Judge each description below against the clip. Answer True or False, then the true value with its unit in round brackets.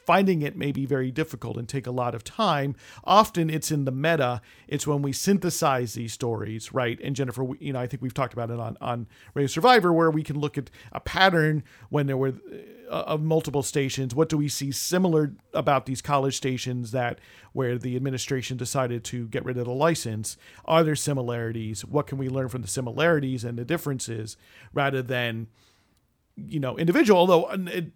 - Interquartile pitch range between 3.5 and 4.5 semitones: True (3.8 semitones)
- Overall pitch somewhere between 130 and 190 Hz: True (135 Hz)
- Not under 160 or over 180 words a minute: False (195 wpm)